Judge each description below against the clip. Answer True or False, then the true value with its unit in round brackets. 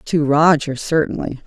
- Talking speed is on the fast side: False (125 wpm)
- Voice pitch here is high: False (150 Hz)